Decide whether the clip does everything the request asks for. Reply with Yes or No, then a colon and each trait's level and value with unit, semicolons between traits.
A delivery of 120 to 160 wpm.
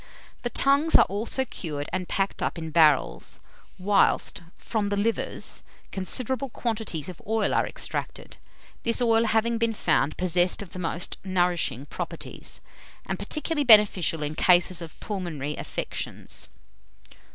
Yes: slow, 135 wpm